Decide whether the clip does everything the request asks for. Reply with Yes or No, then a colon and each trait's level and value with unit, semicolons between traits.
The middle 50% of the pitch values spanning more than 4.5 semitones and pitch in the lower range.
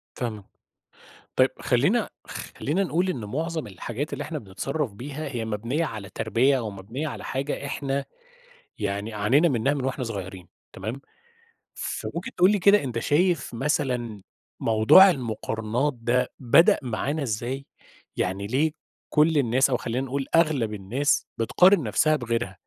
Yes: average, 5.0 semitones; low, 130 Hz